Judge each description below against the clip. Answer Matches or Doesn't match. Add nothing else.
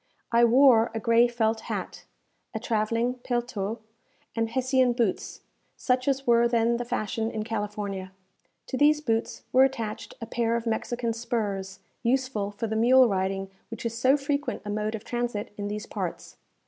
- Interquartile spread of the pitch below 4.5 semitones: Matches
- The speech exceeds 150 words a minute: Matches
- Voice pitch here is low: Doesn't match